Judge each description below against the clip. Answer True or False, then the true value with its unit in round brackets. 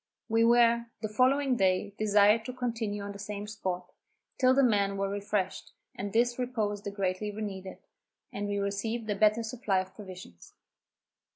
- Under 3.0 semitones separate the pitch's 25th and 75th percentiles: True (2.6 semitones)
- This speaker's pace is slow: False (165 wpm)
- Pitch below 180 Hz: False (210 Hz)